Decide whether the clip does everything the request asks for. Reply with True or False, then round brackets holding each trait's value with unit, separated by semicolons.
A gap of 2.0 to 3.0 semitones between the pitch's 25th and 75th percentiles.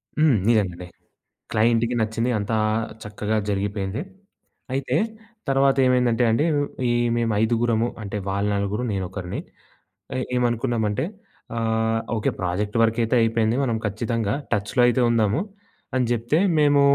True (2.6 semitones)